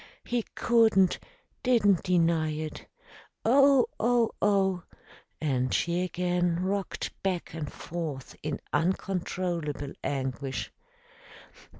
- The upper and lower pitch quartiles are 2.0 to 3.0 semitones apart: No, average, 4.4 semitones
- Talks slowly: Yes, slow, 90 wpm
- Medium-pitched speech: Yes, medium, 180 Hz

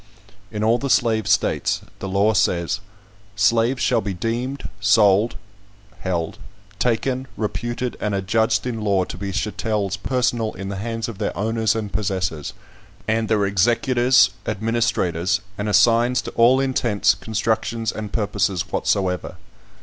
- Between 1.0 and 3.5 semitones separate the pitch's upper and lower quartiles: Yes, average, 2.9 semitones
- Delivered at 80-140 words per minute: Yes, slow, 135 wpm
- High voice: No, low, 110 Hz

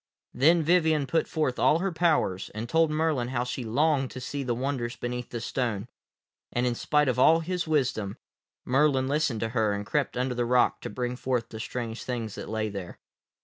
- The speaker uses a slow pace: No, average, 200 wpm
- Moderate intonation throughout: Yes, average, 4.2 semitones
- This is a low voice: Yes, low, 125 Hz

